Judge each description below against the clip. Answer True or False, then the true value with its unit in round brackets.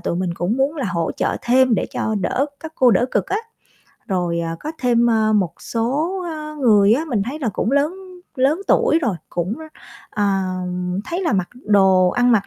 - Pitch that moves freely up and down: True (6.4 semitones)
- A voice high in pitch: True (235 Hz)